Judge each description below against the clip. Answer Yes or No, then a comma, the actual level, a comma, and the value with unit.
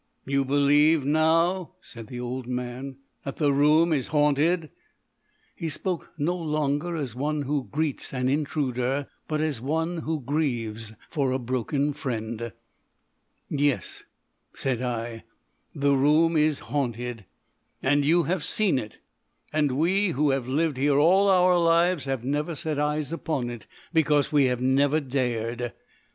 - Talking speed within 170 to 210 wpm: No, average, 145 wpm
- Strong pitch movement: No, average, 3.6 semitones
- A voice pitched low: No, medium, 145 Hz